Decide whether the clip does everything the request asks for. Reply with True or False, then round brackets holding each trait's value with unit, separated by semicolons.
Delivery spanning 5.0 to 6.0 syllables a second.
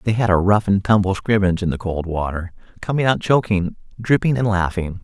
True (5.7 syllables/s)